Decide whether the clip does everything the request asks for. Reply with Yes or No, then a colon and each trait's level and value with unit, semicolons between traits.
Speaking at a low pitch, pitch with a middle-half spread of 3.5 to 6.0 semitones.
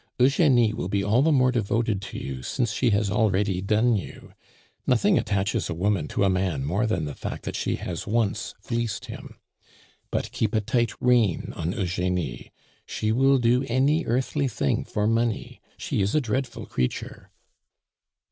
Yes: low, 110 Hz; average, 4.2 semitones